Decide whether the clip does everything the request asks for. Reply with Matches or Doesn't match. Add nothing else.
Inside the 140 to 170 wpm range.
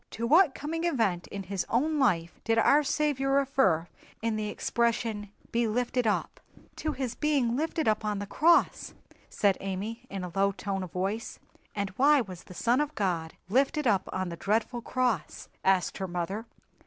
Doesn't match